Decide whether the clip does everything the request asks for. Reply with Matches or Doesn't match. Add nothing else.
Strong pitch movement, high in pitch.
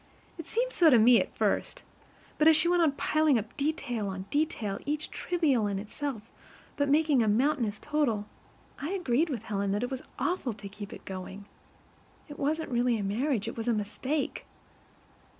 Matches